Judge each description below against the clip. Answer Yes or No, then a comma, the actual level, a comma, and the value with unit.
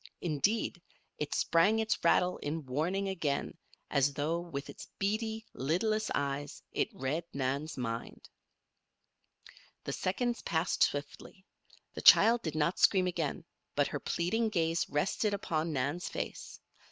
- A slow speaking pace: Yes, slow, 130 wpm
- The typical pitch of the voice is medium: Yes, medium, 165 Hz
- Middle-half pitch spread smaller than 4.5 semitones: No, average, 5.3 semitones